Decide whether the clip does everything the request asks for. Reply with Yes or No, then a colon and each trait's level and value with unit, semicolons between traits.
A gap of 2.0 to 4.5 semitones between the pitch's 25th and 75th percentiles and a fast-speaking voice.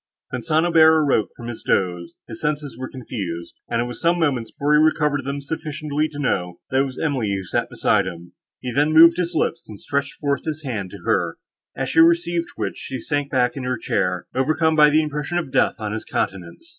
No: average, 5.0 semitones; fast, 220 wpm